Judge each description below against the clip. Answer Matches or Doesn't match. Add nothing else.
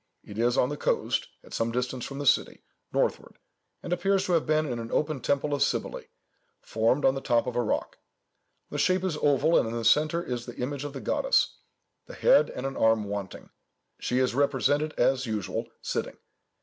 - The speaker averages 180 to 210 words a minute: Matches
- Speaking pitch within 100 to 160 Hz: Matches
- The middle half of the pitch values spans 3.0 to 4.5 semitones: Matches